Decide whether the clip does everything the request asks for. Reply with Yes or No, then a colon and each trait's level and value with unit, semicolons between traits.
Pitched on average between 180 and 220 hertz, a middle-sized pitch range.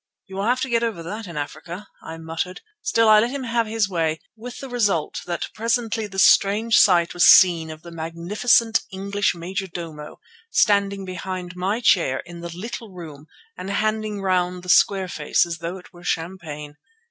Yes: high, 190 Hz; average, 4.1 semitones